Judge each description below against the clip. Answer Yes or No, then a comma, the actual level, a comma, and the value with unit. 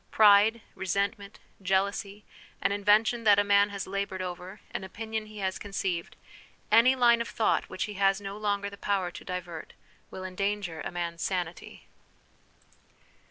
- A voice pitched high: Yes, high, 200 Hz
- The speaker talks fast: No, average, 155 wpm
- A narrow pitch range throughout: Yes, narrow, 1.8 semitones